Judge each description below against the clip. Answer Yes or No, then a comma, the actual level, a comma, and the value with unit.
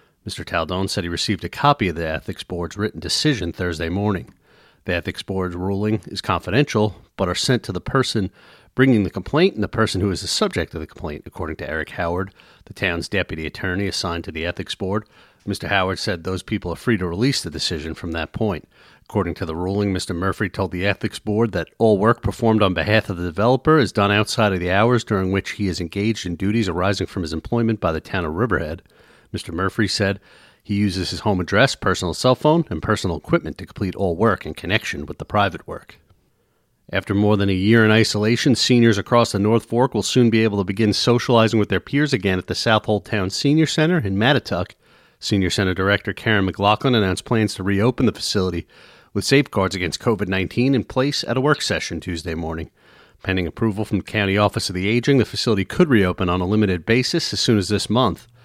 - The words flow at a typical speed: No, fast, 215 wpm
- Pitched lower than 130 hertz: Yes, low, 100 Hz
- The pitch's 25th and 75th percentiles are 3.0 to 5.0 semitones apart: Yes, average, 3.4 semitones